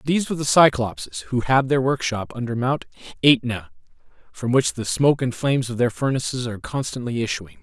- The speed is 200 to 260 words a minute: No, average, 180 wpm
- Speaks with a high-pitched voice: No, low, 125 Hz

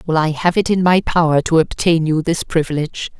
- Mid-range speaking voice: Yes, medium, 165 Hz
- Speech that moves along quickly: Yes, fast, 225 wpm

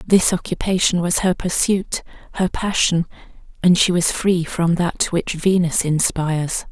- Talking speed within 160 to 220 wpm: No, average, 145 wpm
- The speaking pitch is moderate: Yes, medium, 175 Hz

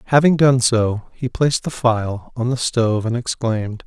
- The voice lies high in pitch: No, low, 120 Hz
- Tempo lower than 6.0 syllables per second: Yes, 4.8 syllables/s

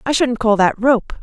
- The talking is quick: Yes, fast, 245 wpm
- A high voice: Yes, high, 235 Hz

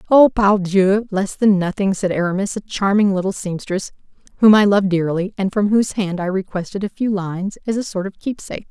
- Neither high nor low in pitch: No, high, 195 Hz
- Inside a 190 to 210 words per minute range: Yes, average, 200 wpm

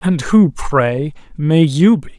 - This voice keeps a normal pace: Yes, average, 165 wpm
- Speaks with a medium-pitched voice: Yes, medium, 160 Hz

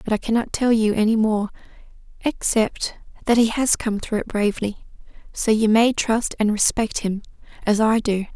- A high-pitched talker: Yes, high, 220 Hz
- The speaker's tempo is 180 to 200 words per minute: No, average, 170 wpm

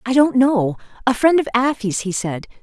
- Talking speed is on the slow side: No, fast, 205 wpm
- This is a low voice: No, high, 235 Hz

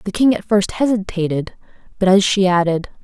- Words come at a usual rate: Yes, average, 180 wpm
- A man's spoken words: No, female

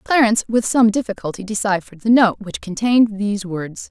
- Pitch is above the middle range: Yes, high, 210 Hz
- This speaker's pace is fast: No, average, 170 wpm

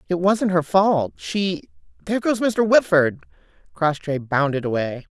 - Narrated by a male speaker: No, female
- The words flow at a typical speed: No, slow, 130 wpm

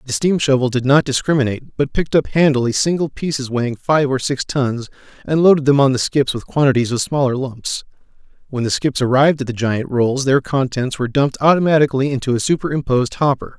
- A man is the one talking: Yes, male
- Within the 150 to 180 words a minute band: No, average, 200 wpm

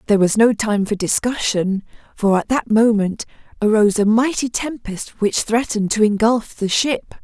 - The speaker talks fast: No, average, 165 wpm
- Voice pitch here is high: Yes, high, 220 Hz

